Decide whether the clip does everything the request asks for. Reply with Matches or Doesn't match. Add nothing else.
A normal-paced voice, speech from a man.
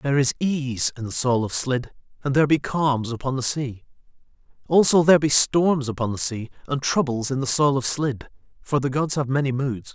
Doesn't match